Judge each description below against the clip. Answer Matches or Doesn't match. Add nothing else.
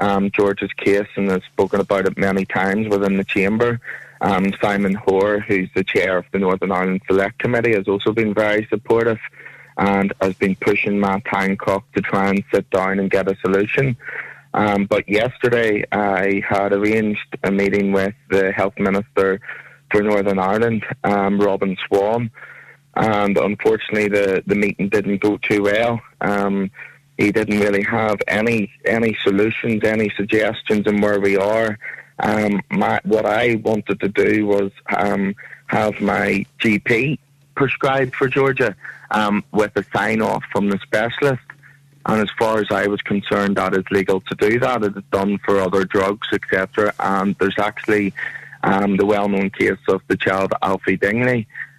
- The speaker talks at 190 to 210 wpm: Doesn't match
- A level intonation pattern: Matches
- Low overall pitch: Matches